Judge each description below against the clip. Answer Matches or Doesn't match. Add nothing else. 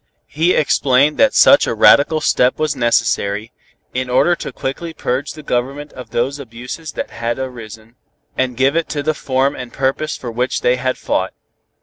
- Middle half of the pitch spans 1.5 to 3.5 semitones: Matches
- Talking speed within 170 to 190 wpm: Matches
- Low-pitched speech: Matches